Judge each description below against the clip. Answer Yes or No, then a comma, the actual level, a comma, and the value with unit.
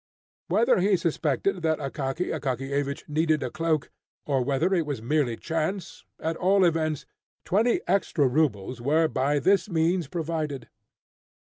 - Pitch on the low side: No, medium, 155 Hz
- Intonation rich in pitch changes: No, average, 3.5 semitones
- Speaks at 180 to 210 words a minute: No, slow, 135 wpm